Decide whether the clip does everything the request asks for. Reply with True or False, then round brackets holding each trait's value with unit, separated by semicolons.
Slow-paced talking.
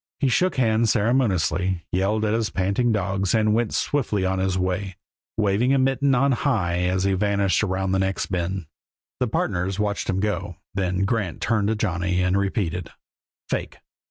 False (170 wpm)